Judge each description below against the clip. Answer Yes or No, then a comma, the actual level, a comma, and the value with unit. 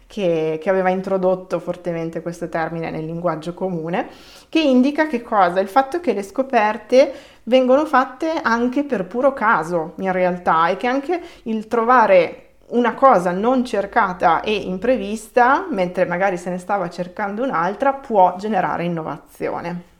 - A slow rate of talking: No, average, 145 wpm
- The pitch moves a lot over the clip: Yes, wide, 6.2 semitones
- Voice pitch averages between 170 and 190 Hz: No, high, 205 Hz